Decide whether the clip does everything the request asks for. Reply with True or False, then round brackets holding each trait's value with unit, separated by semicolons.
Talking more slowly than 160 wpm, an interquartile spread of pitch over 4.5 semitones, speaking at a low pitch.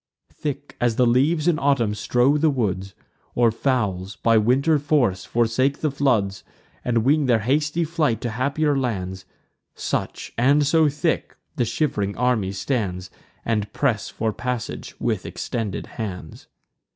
True (140 wpm; 5.0 semitones; 125 Hz)